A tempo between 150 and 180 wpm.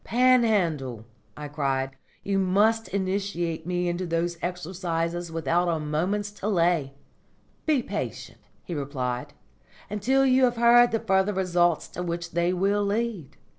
No: slow, 135 wpm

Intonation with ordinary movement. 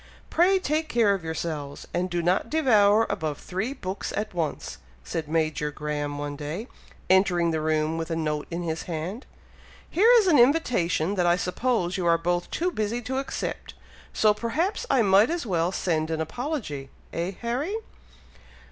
No: wide, 6.8 semitones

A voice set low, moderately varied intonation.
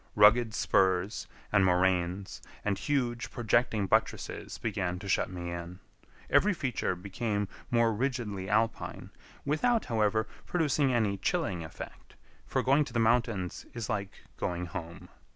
Yes: low, 105 Hz; average, 4.3 semitones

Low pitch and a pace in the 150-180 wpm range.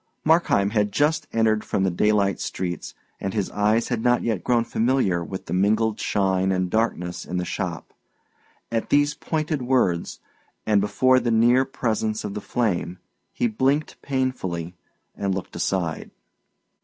Yes: low, 110 Hz; average, 155 wpm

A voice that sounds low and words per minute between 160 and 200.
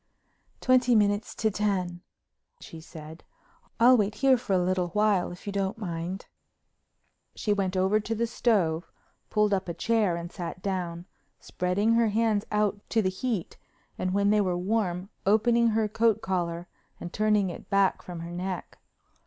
No: high, 200 Hz; average, 165 wpm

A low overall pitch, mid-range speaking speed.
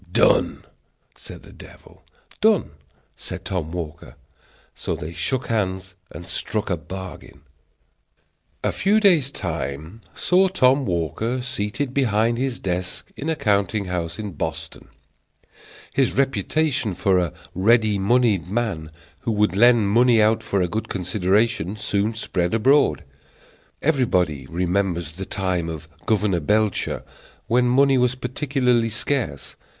No: low, 105 Hz; slow, 130 wpm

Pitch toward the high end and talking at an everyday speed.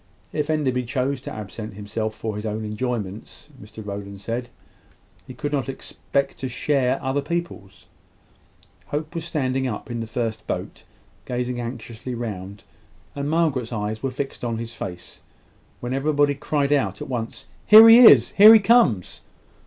No: low, 125 Hz; average, 160 wpm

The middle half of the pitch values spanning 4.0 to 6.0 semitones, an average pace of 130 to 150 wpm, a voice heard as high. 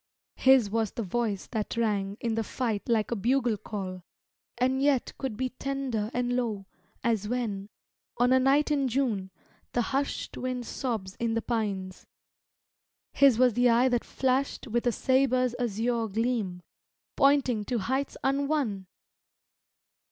No: average, 3.4 semitones; average, 145 wpm; high, 240 Hz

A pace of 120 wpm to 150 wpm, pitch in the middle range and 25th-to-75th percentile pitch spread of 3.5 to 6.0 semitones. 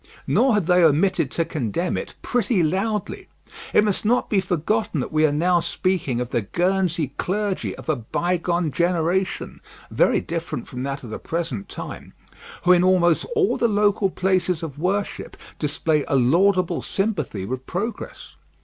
No: average, 160 wpm; medium, 175 Hz; average, 4.1 semitones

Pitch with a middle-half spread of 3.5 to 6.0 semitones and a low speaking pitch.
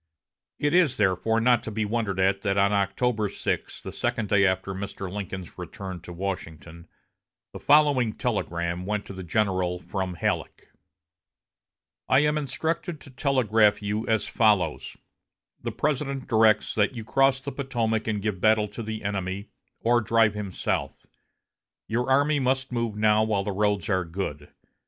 Yes: average, 3.8 semitones; low, 105 Hz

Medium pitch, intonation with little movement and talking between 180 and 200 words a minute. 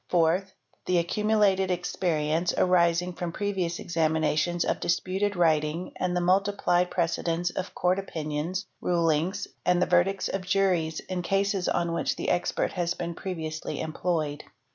No: medium, 175 Hz; narrow, 2.1 semitones; average, 140 wpm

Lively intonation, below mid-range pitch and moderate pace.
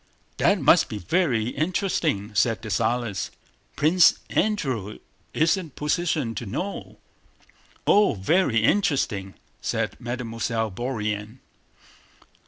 No: wide, 7.0 semitones; low, 120 Hz; slow, 100 wpm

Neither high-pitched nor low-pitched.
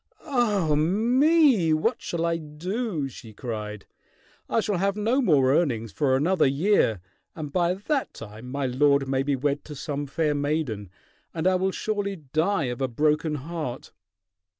Yes: medium, 155 Hz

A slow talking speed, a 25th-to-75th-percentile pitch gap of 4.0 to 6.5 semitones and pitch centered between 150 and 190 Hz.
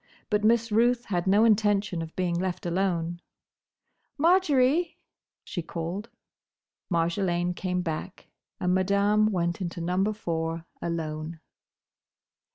No: slow, 110 wpm; average, 3.6 semitones; medium, 185 Hz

